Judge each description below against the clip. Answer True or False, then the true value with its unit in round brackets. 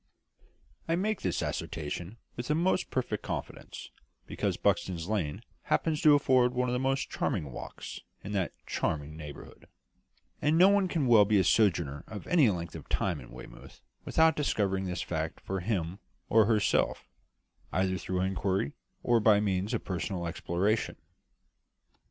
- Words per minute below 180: True (155 wpm)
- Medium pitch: False (100 Hz)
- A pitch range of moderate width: False (6.3 semitones)